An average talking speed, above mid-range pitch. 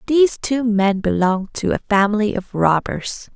Yes: average, 160 wpm; high, 210 Hz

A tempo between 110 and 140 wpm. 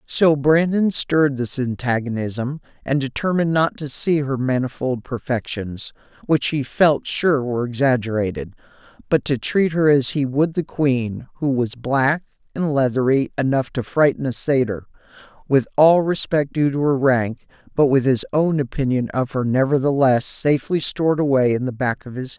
No: average, 160 wpm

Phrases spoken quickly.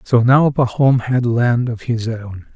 No: average, 190 wpm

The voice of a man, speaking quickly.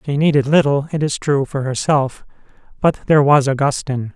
No: male; average, 175 wpm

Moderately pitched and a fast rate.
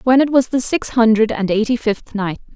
No: high, 230 Hz; fast, 235 wpm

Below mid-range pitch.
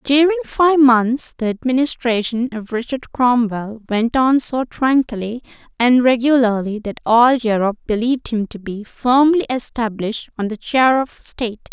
No: high, 240 Hz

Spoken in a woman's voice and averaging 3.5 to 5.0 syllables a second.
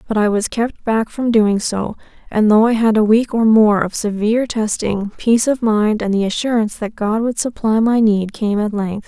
Yes: female; 4.9 syllables/s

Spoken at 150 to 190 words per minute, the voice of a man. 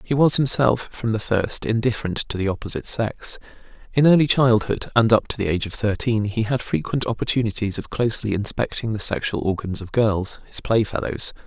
Yes: average, 185 wpm; male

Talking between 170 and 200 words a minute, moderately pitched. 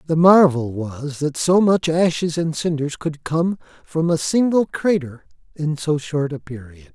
Yes: average, 175 wpm; medium, 155 Hz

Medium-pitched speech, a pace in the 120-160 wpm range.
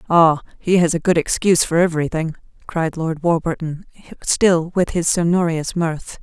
Yes: medium, 165 Hz; average, 155 wpm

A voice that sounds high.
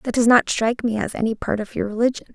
Yes: high, 225 Hz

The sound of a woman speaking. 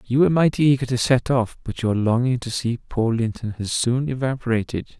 No: male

